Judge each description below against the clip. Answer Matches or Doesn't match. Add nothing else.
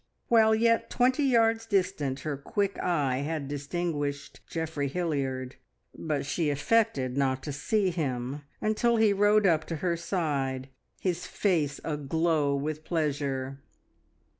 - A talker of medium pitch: Matches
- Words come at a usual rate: Doesn't match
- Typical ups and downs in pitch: Doesn't match